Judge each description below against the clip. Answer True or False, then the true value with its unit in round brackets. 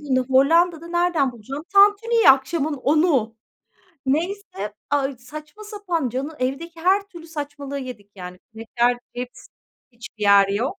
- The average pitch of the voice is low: False (280 Hz)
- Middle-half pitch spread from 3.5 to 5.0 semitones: False (5.5 semitones)